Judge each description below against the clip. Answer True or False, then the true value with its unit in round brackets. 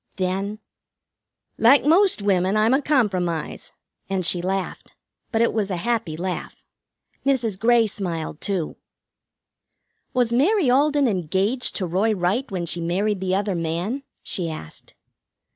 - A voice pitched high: True (200 Hz)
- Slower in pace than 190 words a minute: True (135 wpm)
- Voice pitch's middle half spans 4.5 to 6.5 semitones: True (4.9 semitones)